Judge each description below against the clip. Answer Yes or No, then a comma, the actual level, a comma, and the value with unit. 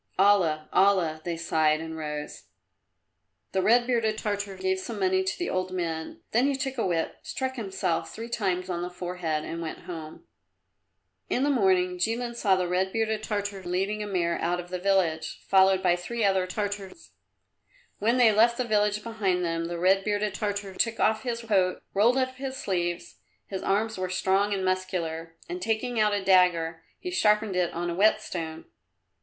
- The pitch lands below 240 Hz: Yes, high, 190 Hz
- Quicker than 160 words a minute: Yes, average, 185 wpm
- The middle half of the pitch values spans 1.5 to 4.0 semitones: Yes, average, 3.5 semitones